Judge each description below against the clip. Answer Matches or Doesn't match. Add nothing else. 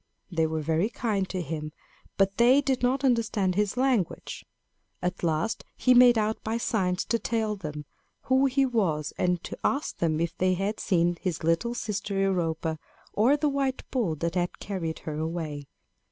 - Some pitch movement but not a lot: Doesn't match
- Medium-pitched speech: Doesn't match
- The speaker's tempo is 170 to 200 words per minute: Matches